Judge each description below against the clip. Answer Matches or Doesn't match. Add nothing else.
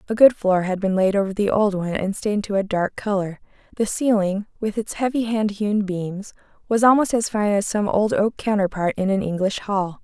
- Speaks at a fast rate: Matches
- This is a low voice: Doesn't match